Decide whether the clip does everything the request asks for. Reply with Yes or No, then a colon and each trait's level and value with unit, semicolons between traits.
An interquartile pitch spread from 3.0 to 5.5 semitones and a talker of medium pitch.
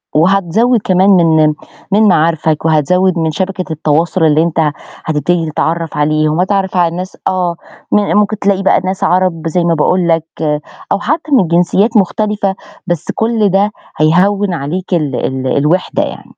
Yes: average, 3.5 semitones; medium, 175 Hz